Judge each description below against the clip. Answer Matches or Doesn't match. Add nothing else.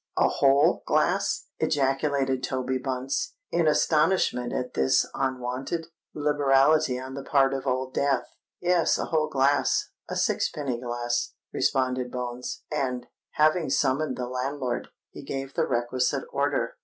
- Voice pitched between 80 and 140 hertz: Matches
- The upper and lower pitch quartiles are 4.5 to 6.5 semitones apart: Doesn't match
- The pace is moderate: Doesn't match